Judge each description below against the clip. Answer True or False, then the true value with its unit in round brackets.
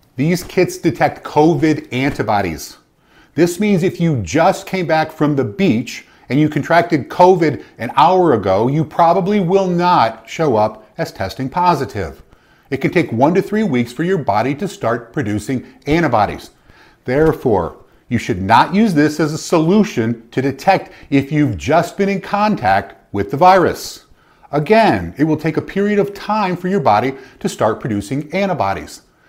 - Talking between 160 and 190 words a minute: True (165 wpm)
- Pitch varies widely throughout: True (6.6 semitones)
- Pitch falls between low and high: True (155 Hz)